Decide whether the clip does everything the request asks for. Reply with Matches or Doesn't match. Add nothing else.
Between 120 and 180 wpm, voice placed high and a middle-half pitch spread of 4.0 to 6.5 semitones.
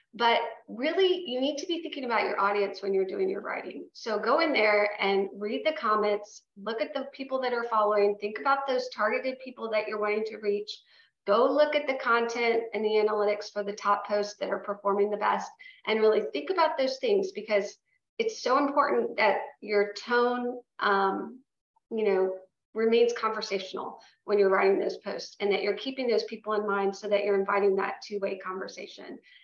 Doesn't match